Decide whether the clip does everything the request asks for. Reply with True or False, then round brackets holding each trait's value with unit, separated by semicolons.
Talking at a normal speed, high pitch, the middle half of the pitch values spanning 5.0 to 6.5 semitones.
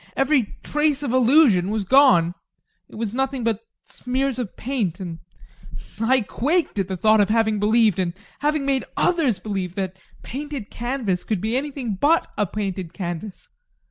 True (165 wpm; 225 Hz; 5.6 semitones)